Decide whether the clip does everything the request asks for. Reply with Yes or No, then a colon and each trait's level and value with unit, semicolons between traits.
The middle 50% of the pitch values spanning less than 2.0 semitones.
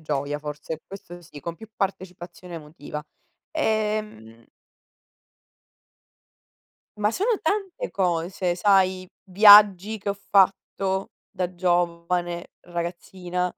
No: average, 2.8 semitones